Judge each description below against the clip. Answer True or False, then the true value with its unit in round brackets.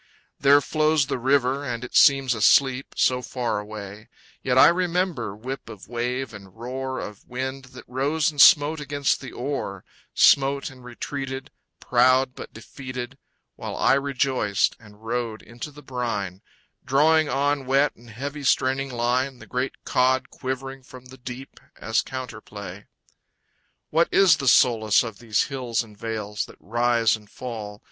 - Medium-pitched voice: False (130 Hz)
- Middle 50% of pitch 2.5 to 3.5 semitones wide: True (2.9 semitones)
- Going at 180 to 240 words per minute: False (155 wpm)